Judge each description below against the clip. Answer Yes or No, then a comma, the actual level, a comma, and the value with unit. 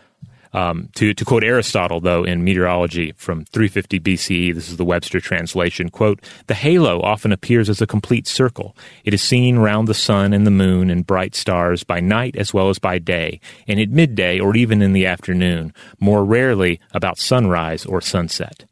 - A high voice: No, very low, 95 Hz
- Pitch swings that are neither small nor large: Yes, average, 3.2 semitones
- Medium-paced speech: Yes, average, 185 wpm